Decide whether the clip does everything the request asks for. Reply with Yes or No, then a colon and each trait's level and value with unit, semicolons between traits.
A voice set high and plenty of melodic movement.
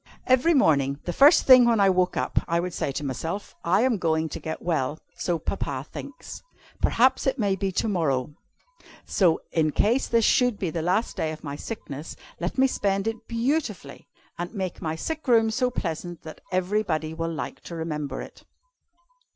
No: medium, 180 Hz; wide, 6.3 semitones